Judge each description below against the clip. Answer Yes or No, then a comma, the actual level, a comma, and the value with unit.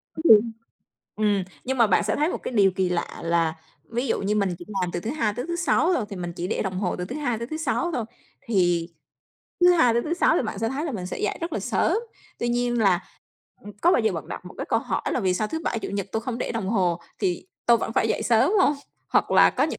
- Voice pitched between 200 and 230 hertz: Yes, high, 220 Hz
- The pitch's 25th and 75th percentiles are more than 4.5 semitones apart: Yes, average, 5.2 semitones